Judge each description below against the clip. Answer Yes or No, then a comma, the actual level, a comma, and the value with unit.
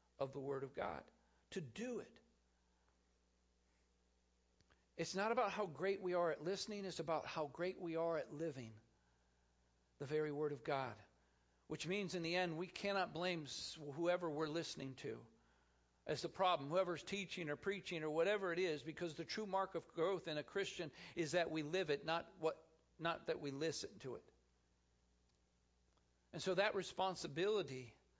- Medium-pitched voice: Yes, medium, 155 Hz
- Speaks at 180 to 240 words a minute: No, average, 170 wpm